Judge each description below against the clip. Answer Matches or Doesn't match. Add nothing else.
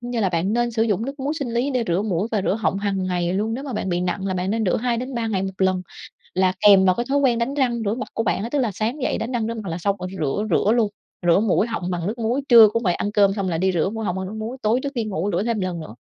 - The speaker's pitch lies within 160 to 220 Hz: Matches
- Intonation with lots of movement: Doesn't match